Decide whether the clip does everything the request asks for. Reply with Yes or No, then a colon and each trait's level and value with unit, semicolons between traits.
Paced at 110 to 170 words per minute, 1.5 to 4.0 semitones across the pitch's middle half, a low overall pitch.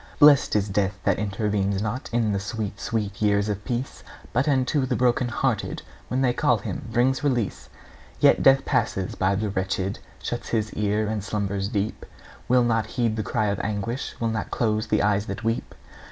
No: average, 185 wpm; average, 3.0 semitones; low, 110 Hz